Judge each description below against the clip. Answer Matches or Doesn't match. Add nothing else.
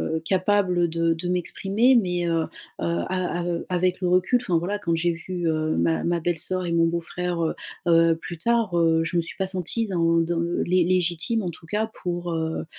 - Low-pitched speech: Doesn't match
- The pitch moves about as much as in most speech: Doesn't match